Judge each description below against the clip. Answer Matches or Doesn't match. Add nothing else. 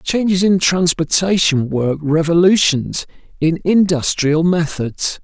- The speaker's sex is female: Doesn't match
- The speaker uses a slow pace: Matches